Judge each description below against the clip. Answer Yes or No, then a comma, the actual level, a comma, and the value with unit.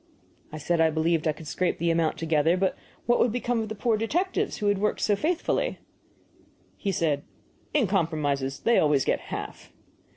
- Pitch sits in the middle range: Yes, medium, 175 Hz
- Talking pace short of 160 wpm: No, average, 185 wpm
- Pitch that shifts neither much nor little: No, wide, 5.9 semitones